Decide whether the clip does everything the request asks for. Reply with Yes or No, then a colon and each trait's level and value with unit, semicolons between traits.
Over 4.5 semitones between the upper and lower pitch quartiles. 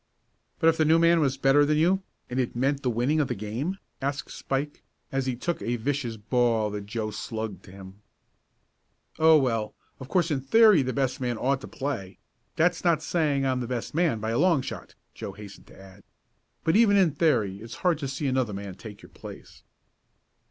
Yes: wide, 5.6 semitones